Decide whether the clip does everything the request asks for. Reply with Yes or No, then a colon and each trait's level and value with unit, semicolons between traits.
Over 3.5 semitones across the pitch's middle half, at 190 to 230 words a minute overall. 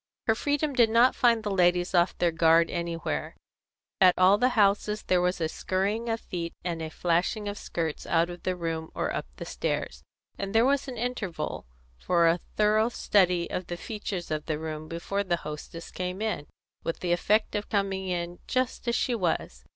Yes: average, 4.2 semitones; average, 195 wpm